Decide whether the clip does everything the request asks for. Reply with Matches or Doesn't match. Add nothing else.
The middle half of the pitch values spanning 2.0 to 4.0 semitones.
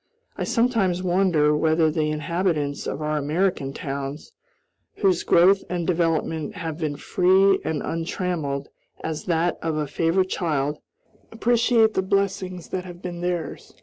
Matches